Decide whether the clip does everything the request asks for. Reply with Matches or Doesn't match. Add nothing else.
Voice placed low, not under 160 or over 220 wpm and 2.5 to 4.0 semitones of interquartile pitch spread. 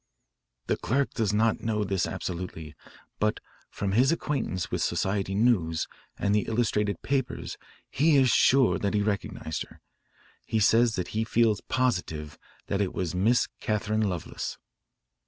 Doesn't match